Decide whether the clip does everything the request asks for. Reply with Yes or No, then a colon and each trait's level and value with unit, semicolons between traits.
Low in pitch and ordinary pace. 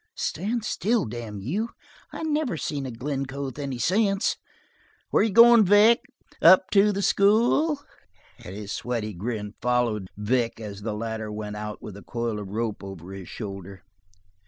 Yes: low, 120 Hz; average, 160 wpm